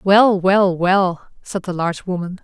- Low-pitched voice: No, medium, 185 Hz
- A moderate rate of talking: Yes, average, 175 wpm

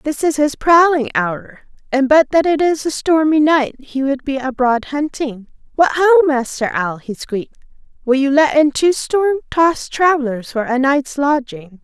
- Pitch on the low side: No, very high, 280 Hz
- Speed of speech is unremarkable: Yes, average, 175 wpm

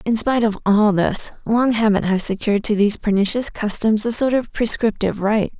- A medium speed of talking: Yes, average, 195 wpm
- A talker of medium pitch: No, high, 215 Hz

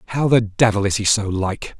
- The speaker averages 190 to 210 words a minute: No, fast, 235 wpm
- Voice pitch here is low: Yes, low, 110 Hz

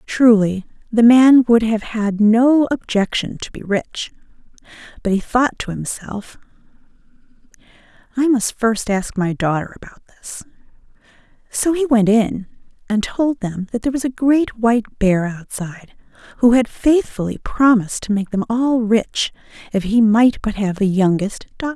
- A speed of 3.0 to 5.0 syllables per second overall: Yes, 4.6 syllables/s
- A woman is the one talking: Yes, female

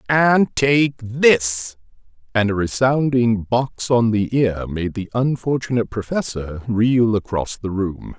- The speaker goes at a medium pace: No, slow, 130 wpm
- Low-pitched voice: Yes, low, 115 Hz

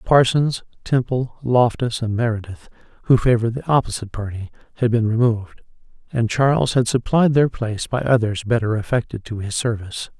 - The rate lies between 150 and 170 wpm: Yes, average, 155 wpm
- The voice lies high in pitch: No, low, 115 Hz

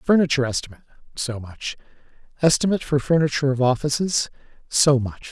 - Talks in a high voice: No, medium, 140 Hz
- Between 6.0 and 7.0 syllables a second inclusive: Yes, 6.4 syllables/s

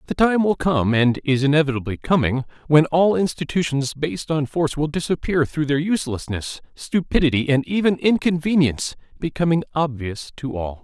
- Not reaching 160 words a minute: Yes, average, 150 wpm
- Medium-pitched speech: Yes, medium, 150 Hz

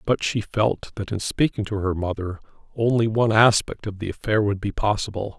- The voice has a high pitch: No, low, 105 Hz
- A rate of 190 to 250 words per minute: Yes, average, 200 wpm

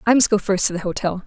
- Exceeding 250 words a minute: Yes, fast, 335 wpm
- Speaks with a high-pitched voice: Yes, high, 200 Hz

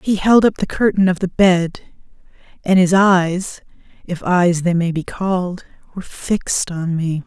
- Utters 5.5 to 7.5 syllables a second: No, 4.4 syllables/s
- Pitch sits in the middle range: Yes, medium, 180 Hz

